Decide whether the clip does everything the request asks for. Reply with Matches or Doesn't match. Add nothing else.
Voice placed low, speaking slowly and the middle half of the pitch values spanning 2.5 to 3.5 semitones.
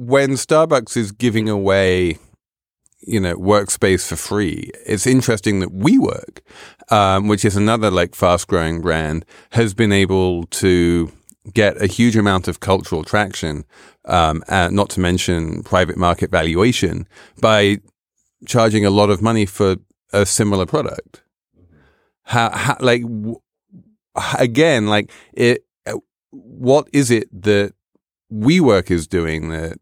Doesn't match